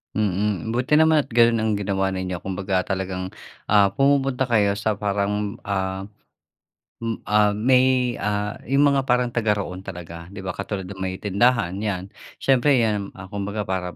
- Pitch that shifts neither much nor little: Yes, average, 3.7 semitones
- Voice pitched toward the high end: No, low, 105 Hz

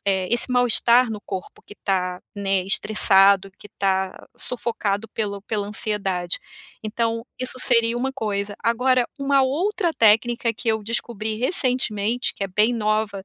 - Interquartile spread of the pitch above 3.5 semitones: No, average, 3.2 semitones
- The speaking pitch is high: Yes, high, 220 Hz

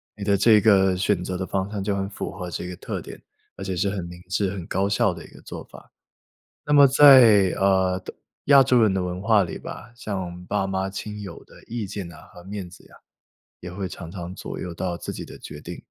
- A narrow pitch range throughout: Yes, narrow, 2.3 semitones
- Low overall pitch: Yes, very low, 95 Hz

